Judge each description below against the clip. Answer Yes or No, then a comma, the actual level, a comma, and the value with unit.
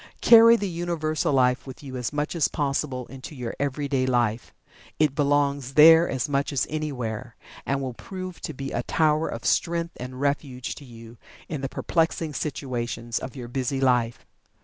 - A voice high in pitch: No, medium, 140 Hz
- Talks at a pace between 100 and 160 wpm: No, average, 170 wpm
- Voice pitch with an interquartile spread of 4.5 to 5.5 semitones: No, average, 3.5 semitones